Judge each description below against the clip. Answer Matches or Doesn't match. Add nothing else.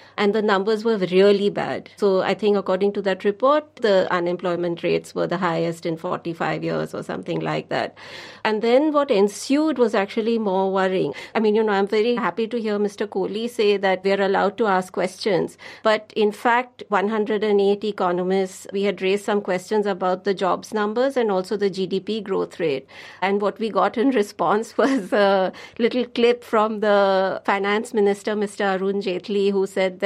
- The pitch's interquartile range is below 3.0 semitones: Matches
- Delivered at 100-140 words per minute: Doesn't match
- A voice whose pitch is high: Matches